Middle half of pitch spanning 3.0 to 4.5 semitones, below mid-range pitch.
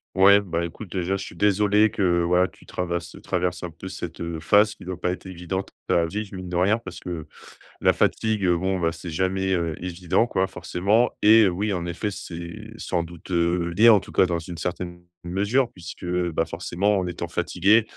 No: narrow, 2.5 semitones; very low, 90 Hz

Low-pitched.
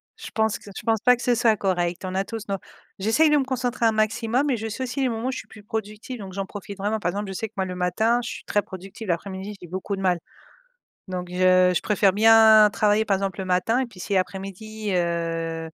No: high, 205 Hz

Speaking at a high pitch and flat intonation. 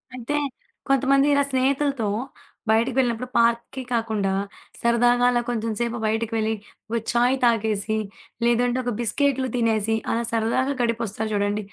Yes: high, 235 Hz; narrow, 2.2 semitones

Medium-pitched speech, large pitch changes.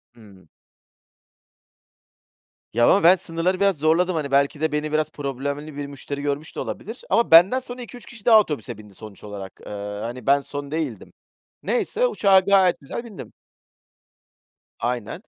Yes: medium, 155 Hz; wide, 5.7 semitones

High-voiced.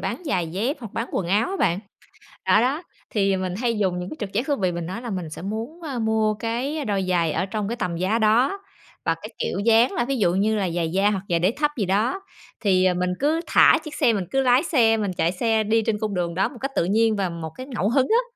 Yes: high, 215 Hz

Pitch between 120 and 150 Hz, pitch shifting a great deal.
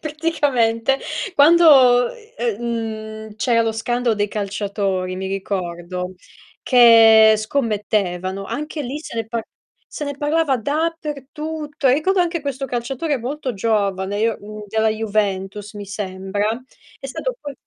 No: high, 230 Hz; wide, 5.8 semitones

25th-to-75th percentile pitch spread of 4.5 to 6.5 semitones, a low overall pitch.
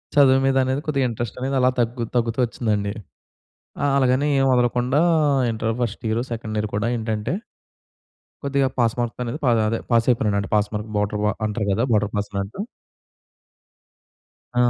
No: average, 3.3 semitones; low, 115 Hz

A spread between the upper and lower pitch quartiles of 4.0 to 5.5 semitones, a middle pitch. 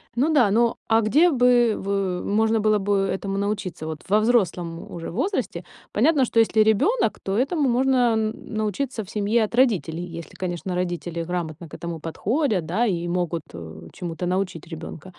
No: average, 5.0 semitones; high, 200 Hz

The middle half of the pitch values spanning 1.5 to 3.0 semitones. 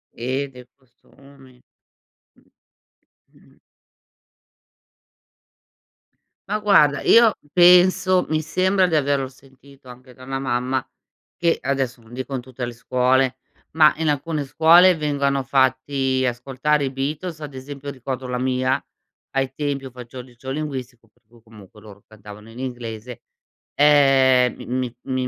Yes: narrow, 2.6 semitones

